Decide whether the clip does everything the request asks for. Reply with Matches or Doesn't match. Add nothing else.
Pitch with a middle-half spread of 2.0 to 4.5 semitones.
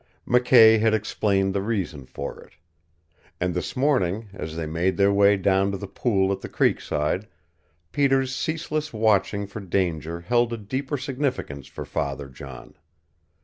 Doesn't match